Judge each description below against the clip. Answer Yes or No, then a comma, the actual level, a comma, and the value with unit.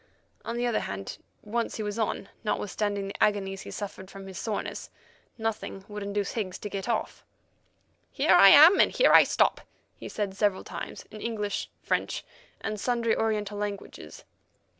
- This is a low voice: No, high, 210 Hz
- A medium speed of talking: Yes, average, 165 wpm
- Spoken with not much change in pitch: Yes, narrow, 2.1 semitones